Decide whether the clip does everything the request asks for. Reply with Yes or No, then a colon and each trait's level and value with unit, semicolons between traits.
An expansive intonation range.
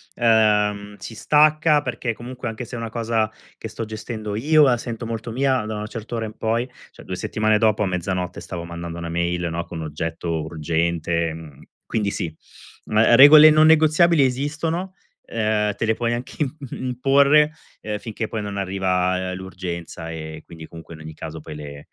Yes: wide, 6.0 semitones